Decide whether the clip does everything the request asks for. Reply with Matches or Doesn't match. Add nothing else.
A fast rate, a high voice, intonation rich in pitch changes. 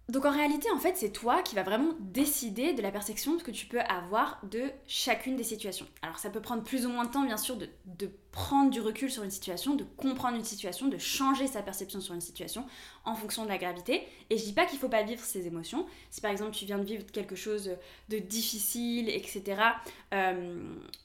Doesn't match